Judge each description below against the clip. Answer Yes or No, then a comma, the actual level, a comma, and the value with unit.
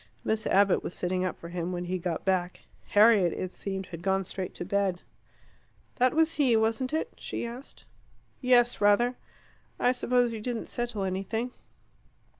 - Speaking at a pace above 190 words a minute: No, average, 165 wpm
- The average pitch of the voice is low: No, high, 205 Hz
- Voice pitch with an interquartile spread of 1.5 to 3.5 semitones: No, average, 4.6 semitones